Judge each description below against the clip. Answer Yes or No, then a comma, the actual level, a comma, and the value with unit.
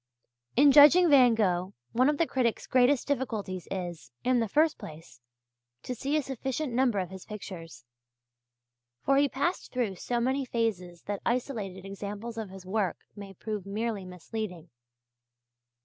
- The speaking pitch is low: No, high, 220 Hz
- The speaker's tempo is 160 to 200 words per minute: No, average, 150 wpm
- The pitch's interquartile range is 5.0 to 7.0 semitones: Yes, wide, 5.6 semitones